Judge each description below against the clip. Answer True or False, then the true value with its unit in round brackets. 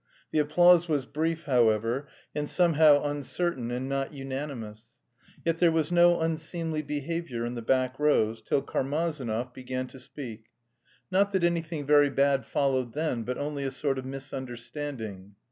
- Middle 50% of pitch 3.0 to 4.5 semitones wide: True (3.8 semitones)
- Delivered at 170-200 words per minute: False (150 wpm)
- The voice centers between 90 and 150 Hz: True (140 Hz)